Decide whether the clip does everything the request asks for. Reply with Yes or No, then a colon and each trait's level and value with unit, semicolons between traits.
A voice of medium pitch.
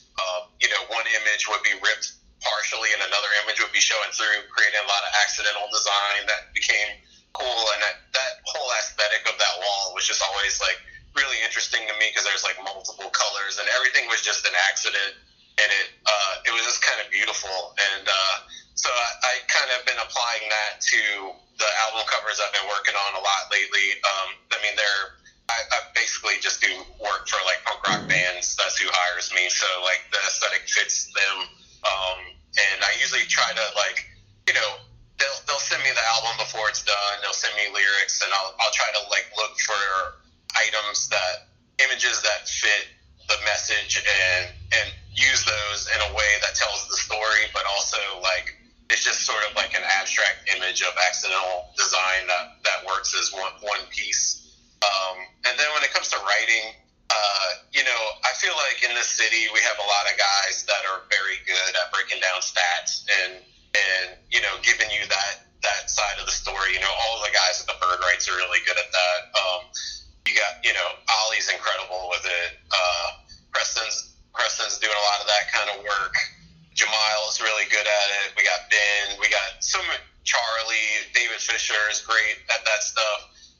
No: low, 100 Hz